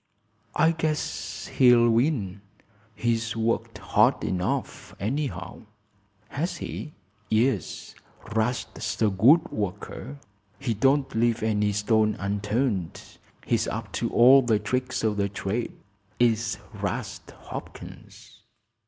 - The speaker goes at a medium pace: No, slow, 110 wpm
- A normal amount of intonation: Yes, average, 3.7 semitones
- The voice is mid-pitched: No, low, 115 Hz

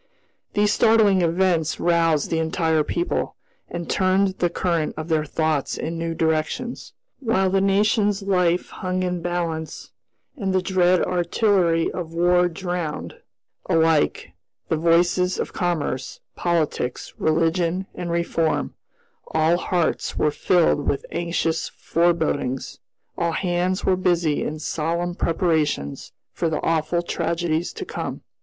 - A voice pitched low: No, medium, 170 Hz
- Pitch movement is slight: Yes, narrow, 2.2 semitones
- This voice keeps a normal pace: No, slow, 130 wpm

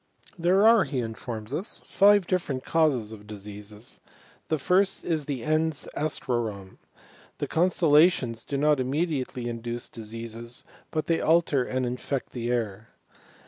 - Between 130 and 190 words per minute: Yes, average, 140 wpm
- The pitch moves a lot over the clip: Yes, wide, 5.7 semitones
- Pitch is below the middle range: Yes, low, 130 Hz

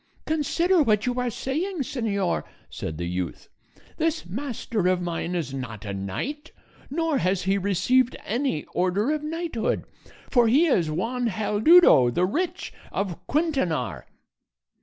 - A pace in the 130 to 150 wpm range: Yes, average, 140 wpm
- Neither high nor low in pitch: No, high, 225 Hz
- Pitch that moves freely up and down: Yes, wide, 8.9 semitones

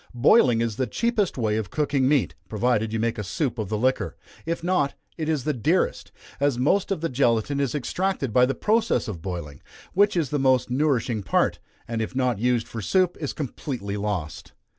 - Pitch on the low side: Yes, low, 130 Hz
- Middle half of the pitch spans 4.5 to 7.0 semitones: Yes, average, 5.3 semitones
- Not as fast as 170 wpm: No, average, 200 wpm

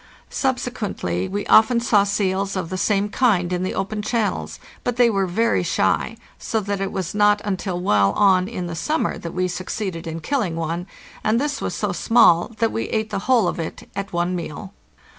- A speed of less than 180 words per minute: No, average, 200 wpm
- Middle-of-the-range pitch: No, high, 195 Hz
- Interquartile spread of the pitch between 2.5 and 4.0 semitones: Yes, average, 3.7 semitones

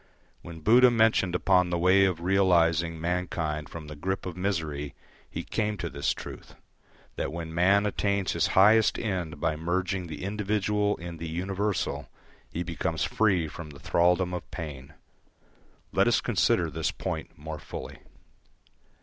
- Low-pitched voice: Yes, very low, 90 Hz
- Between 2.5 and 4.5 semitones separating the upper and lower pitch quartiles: Yes, average, 3.1 semitones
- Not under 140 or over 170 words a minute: Yes, average, 150 wpm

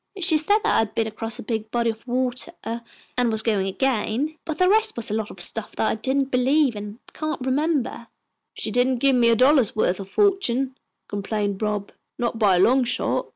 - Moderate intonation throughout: Yes, average, 3.9 semitones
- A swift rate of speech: Yes, fast, 210 wpm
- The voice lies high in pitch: Yes, high, 240 Hz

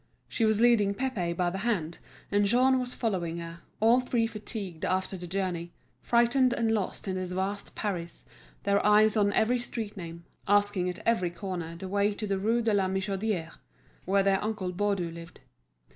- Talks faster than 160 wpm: Yes, average, 180 wpm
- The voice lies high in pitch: Yes, high, 200 Hz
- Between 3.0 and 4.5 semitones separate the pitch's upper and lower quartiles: Yes, average, 3.5 semitones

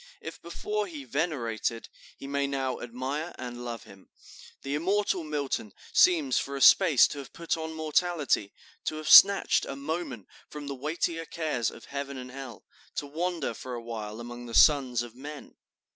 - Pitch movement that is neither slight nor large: Yes, average, 4.6 semitones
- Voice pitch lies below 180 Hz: Yes, medium, 140 Hz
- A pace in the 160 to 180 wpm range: Yes, average, 175 wpm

